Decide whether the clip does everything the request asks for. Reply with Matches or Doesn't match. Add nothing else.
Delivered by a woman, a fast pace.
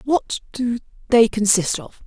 Doesn't match